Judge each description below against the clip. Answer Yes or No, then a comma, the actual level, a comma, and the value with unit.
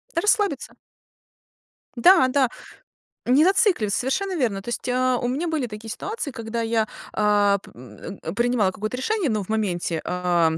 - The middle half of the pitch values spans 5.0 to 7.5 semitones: Yes, wide, 5.6 semitones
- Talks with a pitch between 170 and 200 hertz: No, high, 240 Hz